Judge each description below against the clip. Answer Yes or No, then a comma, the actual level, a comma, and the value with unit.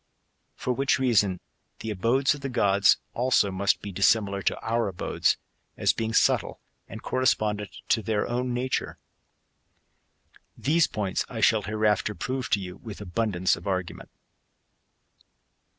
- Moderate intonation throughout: Yes, average, 3.8 semitones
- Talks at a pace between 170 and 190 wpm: No, slow, 135 wpm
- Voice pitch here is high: No, low, 110 Hz